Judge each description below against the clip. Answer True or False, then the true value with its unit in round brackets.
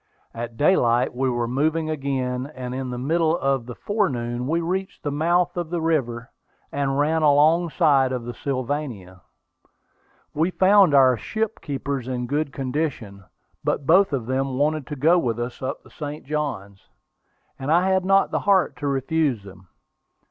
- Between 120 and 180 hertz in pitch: True (140 Hz)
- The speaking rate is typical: True (165 wpm)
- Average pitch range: True (4.3 semitones)